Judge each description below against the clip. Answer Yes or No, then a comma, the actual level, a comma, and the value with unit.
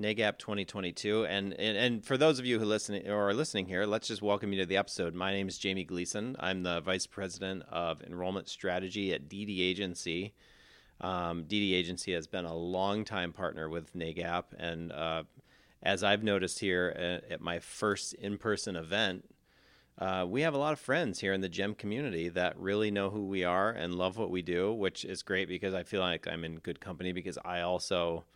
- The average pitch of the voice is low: Yes, very low, 95 Hz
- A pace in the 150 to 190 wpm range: No, fast, 205 wpm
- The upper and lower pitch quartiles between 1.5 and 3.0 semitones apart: Yes, narrow, 2.4 semitones